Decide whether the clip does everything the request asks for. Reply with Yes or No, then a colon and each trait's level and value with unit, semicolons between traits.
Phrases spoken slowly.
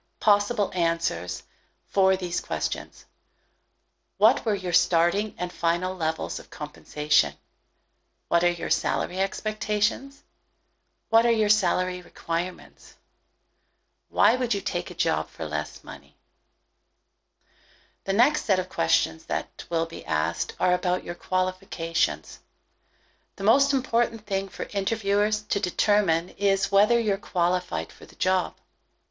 Yes: slow, 125 wpm